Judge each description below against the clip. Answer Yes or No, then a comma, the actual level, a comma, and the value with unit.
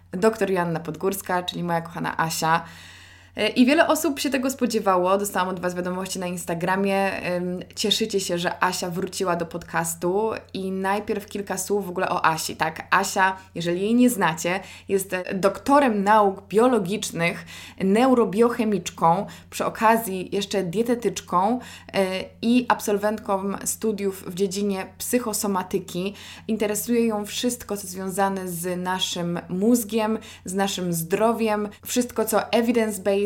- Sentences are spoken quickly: No, average, 125 wpm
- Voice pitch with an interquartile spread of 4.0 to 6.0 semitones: No, average, 3.1 semitones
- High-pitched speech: Yes, high, 195 Hz